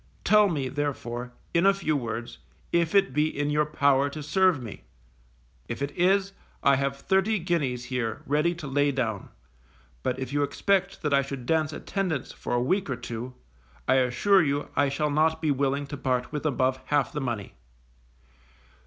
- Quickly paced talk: No, average, 180 wpm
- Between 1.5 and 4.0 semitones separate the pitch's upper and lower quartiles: Yes, average, 3.7 semitones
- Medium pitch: Yes, medium, 145 Hz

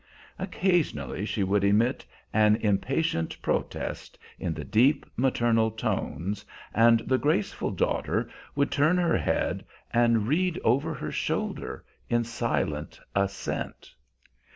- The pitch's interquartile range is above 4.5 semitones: Yes, wide, 5.6 semitones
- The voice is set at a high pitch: No, low, 115 Hz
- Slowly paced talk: Yes, slow, 115 wpm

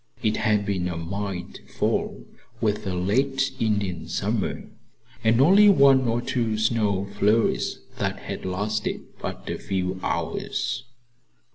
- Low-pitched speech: Yes, low, 105 Hz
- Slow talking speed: Yes, slow, 130 wpm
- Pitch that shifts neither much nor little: Yes, average, 3.6 semitones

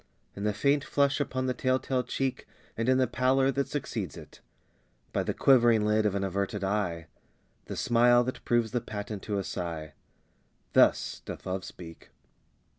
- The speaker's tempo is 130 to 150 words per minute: No, average, 175 wpm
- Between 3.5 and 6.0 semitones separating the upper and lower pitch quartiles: Yes, average, 4.5 semitones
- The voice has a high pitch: No, low, 115 Hz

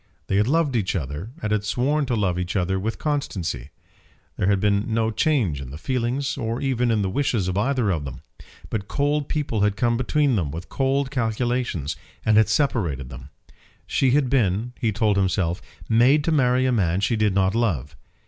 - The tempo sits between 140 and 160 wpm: No, average, 195 wpm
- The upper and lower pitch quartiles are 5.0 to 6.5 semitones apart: Yes, wide, 5.5 semitones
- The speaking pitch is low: Yes, low, 110 Hz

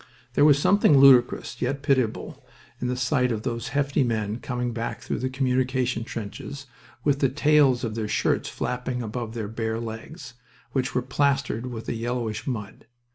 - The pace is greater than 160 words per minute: Yes, average, 170 wpm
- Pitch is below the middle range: Yes, low, 125 Hz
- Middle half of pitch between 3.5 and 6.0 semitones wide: No, average, 2.8 semitones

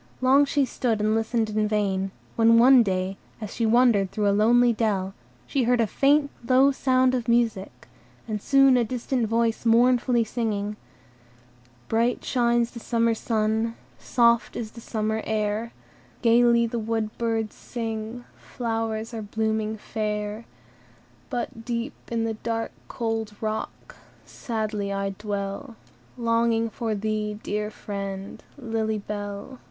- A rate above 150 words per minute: No, average, 140 wpm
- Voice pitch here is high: Yes, high, 225 Hz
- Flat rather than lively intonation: Yes, narrow, 1.9 semitones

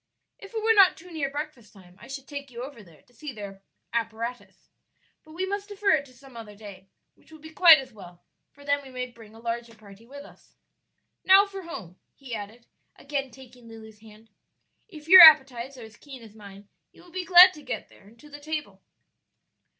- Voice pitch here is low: No, very high, 260 Hz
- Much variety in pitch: Yes, wide, 5.9 semitones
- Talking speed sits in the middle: No, fast, 215 wpm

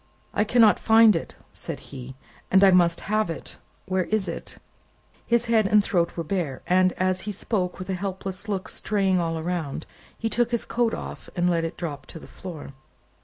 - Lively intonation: No, average, 3.8 semitones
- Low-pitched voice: No, medium, 185 Hz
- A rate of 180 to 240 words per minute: Yes, average, 195 wpm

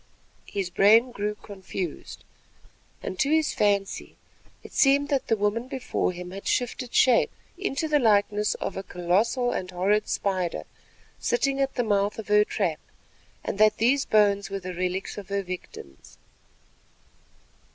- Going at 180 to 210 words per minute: No, average, 150 wpm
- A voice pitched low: No, high, 210 Hz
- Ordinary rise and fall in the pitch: Yes, average, 4.3 semitones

